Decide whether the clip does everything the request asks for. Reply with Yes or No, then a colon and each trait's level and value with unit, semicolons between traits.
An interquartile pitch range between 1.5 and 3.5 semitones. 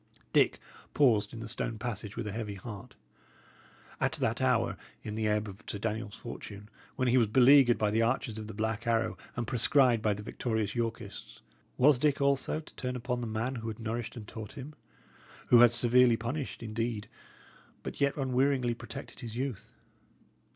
Yes: narrow, 2.6 semitones